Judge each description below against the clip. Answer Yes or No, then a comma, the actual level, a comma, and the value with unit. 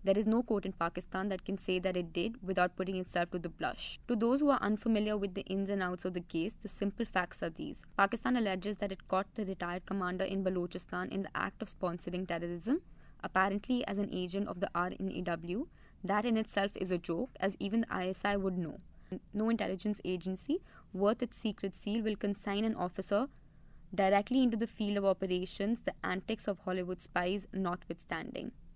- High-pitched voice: Yes, high, 195 Hz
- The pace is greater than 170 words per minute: Yes, average, 195 wpm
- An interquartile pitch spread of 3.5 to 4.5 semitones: No, narrow, 2.5 semitones